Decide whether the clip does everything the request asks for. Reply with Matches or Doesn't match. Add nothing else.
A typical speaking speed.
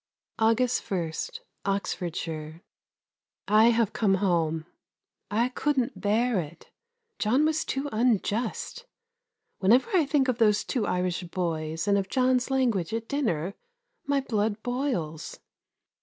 Doesn't match